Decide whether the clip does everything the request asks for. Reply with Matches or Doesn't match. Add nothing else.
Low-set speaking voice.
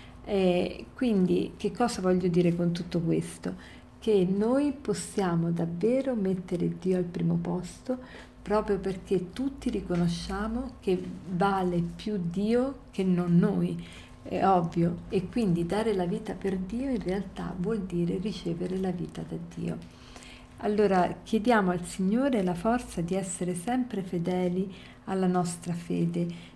Doesn't match